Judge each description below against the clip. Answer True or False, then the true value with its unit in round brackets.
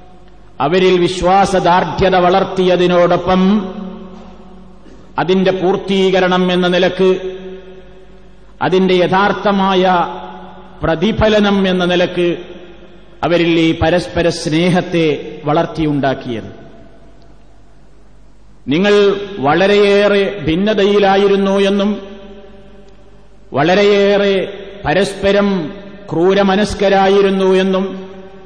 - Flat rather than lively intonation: True (1.9 semitones)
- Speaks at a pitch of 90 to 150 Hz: False (185 Hz)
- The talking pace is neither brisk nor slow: False (55 wpm)